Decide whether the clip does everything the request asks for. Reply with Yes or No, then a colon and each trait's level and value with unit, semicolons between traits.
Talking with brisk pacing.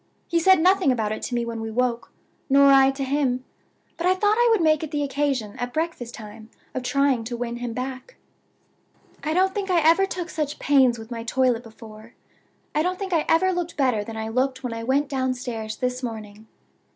Yes: fast, 210 wpm